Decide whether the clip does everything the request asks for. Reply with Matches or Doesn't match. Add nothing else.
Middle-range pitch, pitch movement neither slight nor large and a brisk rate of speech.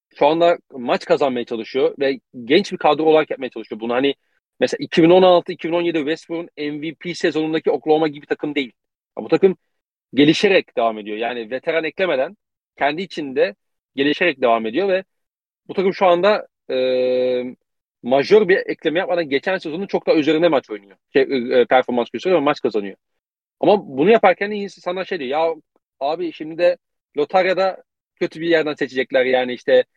Doesn't match